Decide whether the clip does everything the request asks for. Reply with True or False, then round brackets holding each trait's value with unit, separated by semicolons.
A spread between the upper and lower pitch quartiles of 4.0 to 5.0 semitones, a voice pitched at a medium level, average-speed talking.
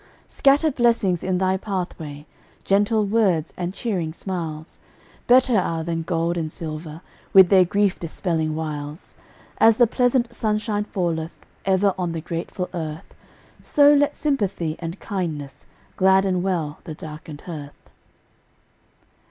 False (4.3 semitones; 180 Hz; 125 wpm)